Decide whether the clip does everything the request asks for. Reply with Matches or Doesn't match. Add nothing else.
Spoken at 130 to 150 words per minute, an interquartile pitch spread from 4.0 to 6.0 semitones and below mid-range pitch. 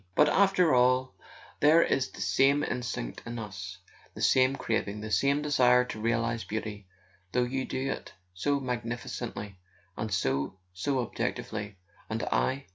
Matches